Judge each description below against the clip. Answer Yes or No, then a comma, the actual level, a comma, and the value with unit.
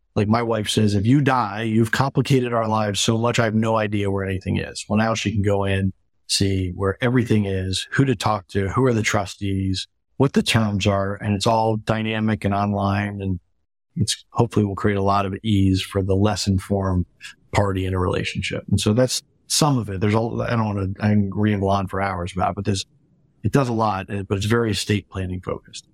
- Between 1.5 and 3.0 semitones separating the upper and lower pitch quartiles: Yes, narrow, 2.5 semitones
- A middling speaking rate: No, fast, 220 wpm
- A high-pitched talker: No, low, 105 Hz